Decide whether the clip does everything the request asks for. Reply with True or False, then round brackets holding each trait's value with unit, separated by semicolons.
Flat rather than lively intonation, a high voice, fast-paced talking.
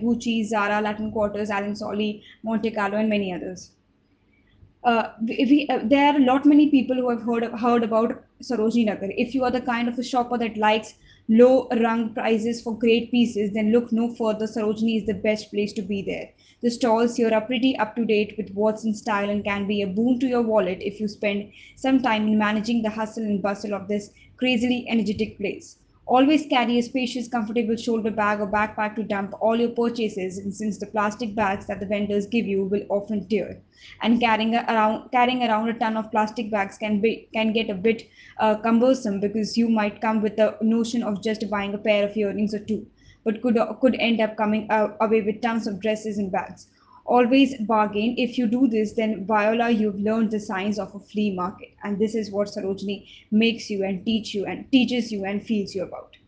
True (2.1 semitones; 220 Hz; 210 wpm)